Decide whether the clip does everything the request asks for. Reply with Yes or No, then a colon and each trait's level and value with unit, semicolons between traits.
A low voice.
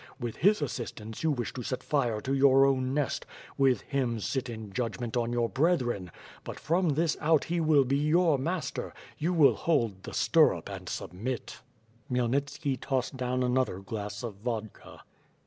Yes: low, 130 Hz